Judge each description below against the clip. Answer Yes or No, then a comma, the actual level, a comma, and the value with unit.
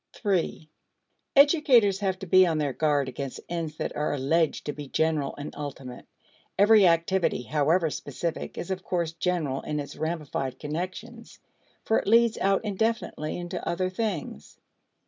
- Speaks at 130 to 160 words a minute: Yes, average, 150 wpm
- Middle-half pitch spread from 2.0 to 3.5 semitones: No, average, 4.5 semitones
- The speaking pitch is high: No, medium, 170 Hz